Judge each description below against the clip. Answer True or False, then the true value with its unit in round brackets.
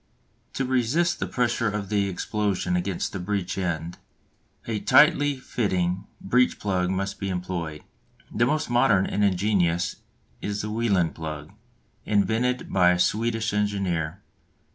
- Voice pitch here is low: True (100 Hz)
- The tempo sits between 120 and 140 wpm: True (135 wpm)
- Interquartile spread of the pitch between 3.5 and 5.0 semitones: True (4.0 semitones)